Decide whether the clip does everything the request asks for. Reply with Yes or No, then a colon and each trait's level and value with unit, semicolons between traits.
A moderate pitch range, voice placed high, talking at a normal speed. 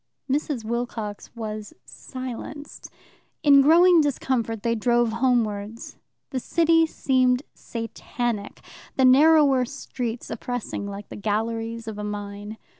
No: average, 3.6 semitones; high, 240 Hz; slow, 115 wpm